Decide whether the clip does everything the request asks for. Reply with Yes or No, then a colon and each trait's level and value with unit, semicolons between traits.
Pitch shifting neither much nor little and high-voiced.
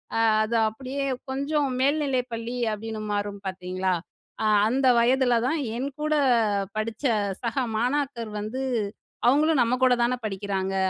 Yes: average, 4.0 semitones; high, 245 Hz